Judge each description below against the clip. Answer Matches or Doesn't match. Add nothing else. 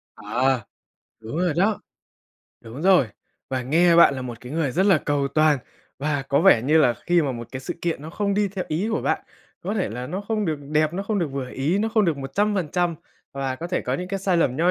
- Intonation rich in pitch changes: Matches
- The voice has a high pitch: Doesn't match